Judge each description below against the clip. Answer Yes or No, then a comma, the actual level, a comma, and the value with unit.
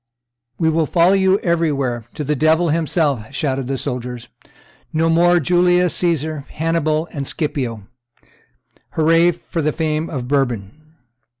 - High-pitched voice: No, medium, 155 Hz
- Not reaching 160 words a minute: Yes, slow, 135 wpm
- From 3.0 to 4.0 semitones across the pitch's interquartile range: Yes, average, 3.5 semitones